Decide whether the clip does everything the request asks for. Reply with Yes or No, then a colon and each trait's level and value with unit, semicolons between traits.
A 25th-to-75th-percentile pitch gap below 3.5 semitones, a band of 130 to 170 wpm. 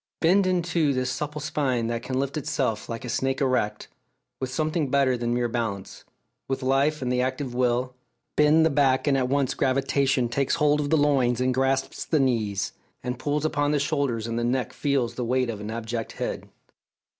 No: average, 3.1 semitones; average, 200 wpm